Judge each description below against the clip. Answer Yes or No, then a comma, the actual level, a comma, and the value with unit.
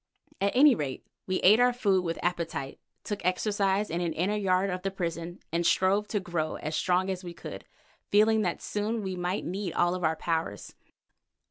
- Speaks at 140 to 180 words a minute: No, average, 190 wpm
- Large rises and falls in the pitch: No, average, 3.0 semitones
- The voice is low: No, medium, 185 Hz